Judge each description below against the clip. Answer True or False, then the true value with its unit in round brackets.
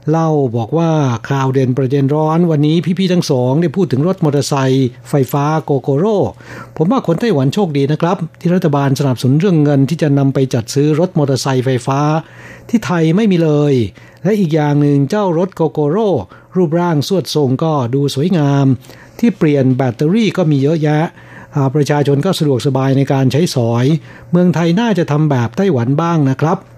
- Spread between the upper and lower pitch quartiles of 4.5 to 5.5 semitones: False (3.7 semitones)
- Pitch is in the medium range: True (150 Hz)